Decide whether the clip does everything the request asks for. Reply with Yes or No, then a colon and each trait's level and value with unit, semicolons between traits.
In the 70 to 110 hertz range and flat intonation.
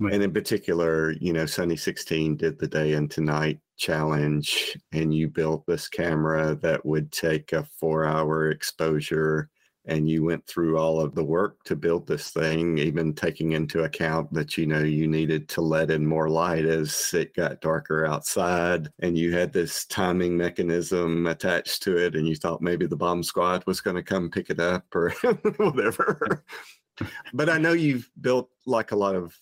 Yes: very low, 80 Hz; narrow, 2.0 semitones